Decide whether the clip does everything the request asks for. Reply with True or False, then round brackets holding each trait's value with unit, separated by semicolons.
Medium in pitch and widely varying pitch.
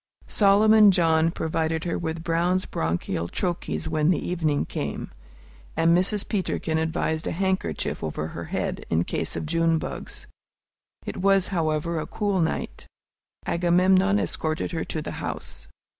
False (165 Hz; 2.8 semitones)